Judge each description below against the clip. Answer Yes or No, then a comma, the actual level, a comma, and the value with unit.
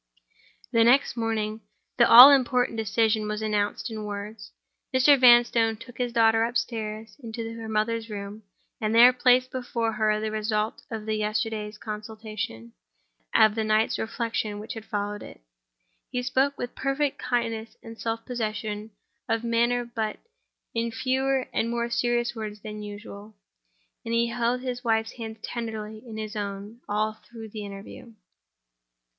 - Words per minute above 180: No, average, 150 wpm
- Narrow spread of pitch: Yes, narrow, 1.9 semitones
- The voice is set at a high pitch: Yes, high, 225 Hz